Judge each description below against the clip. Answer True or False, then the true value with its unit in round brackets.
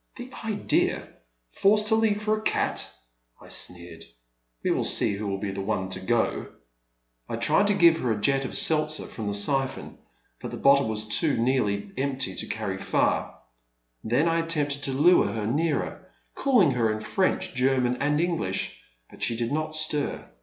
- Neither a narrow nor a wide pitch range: False (7.5 semitones)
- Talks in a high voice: False (135 Hz)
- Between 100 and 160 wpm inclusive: False (185 wpm)